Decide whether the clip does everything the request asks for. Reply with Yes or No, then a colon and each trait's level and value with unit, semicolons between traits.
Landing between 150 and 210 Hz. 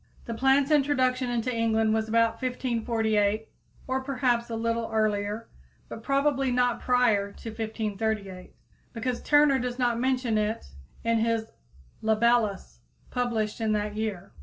No: high, 230 Hz